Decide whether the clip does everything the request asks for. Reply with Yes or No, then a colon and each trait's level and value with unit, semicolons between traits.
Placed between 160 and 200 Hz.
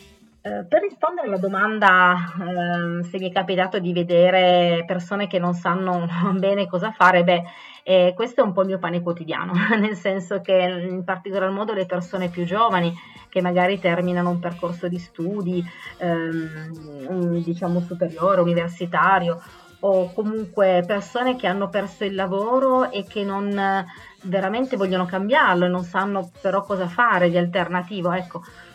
Yes: medium, 185 Hz